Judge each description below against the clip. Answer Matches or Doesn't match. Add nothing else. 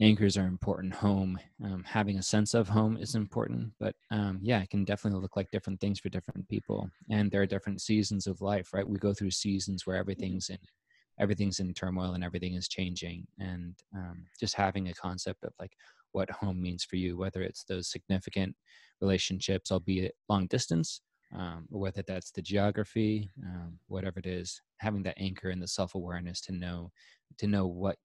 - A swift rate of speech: Doesn't match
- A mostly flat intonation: Matches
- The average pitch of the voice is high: Doesn't match